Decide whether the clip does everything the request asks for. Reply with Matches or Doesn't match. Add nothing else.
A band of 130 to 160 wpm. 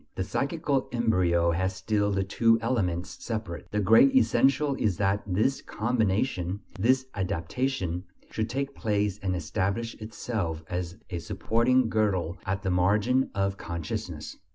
Matches